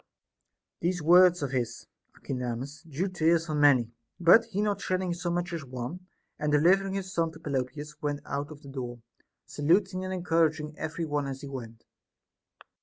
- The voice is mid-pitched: Yes, medium, 155 Hz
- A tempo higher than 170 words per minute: Yes, average, 180 wpm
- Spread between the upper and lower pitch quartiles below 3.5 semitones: No, average, 4.2 semitones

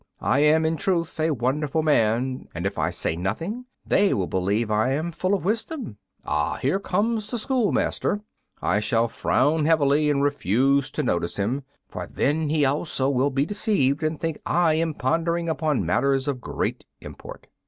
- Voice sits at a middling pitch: Yes, medium, 145 Hz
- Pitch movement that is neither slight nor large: Yes, average, 4.6 semitones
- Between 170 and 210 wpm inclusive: Yes, average, 175 wpm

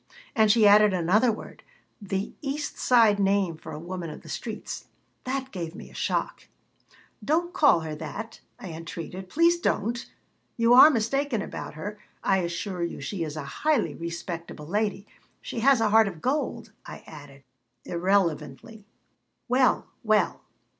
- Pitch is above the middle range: Yes, high, 205 Hz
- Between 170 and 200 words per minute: No, average, 155 wpm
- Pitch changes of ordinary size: No, wide, 5.8 semitones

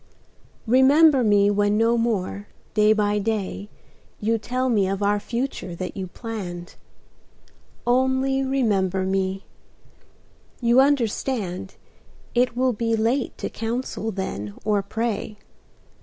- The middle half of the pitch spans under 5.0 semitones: Yes, average, 3.8 semitones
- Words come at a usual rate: No, slow, 115 wpm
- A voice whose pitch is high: Yes, high, 220 Hz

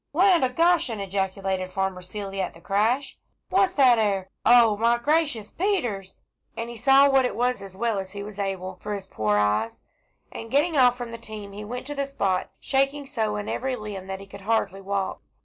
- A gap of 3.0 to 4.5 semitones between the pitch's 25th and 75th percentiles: No, average, 5.0 semitones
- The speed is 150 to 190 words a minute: No, fast, 205 wpm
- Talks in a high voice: Yes, high, 215 Hz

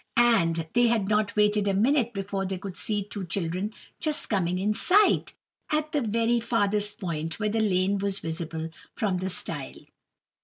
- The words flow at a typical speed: Yes, average, 170 wpm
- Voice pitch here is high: Yes, high, 205 Hz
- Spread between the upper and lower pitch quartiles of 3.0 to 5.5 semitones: Yes, average, 3.6 semitones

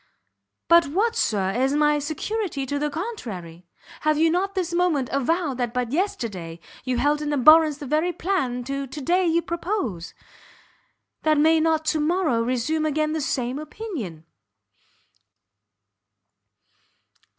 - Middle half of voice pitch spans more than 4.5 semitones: Yes, average, 5.0 semitones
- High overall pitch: Yes, very high, 300 Hz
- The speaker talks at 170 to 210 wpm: No, average, 140 wpm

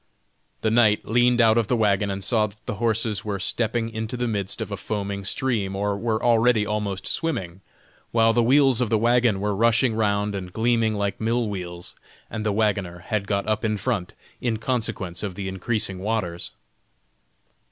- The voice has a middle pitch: No, low, 110 Hz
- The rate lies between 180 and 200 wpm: Yes, average, 185 wpm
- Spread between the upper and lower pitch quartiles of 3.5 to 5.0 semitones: No, narrow, 2.6 semitones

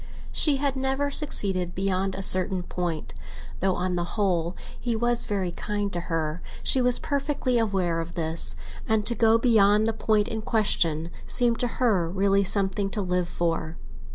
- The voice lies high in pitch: Yes, high, 195 Hz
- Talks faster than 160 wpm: Yes, average, 170 wpm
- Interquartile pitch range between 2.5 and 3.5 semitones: No, average, 4.5 semitones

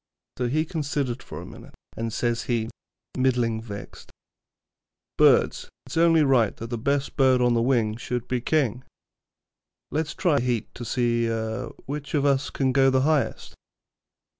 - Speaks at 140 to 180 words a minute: Yes, average, 160 wpm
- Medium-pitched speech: No, low, 130 Hz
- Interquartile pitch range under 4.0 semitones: Yes, average, 3.2 semitones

